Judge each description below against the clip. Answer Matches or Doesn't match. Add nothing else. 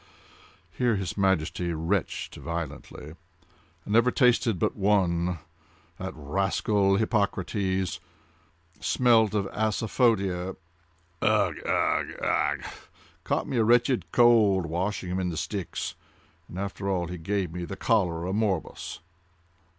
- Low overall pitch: Matches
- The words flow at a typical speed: Doesn't match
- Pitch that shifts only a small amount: Doesn't match